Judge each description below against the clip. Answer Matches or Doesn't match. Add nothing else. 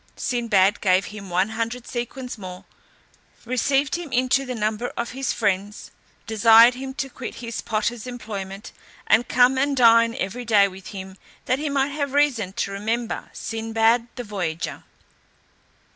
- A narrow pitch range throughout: Doesn't match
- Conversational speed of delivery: Matches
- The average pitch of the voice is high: Matches